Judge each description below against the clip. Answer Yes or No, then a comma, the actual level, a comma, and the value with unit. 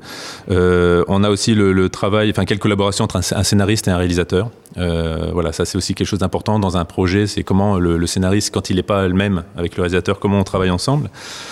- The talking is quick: Yes, fast, 235 wpm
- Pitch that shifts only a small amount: Yes, narrow, 2.2 semitones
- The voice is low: Yes, very low, 95 Hz